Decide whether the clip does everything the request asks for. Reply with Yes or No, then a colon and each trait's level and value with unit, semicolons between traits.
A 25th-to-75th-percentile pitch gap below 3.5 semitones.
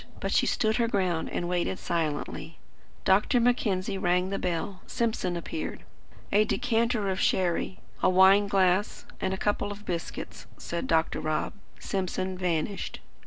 Yes: average, 2.8 semitones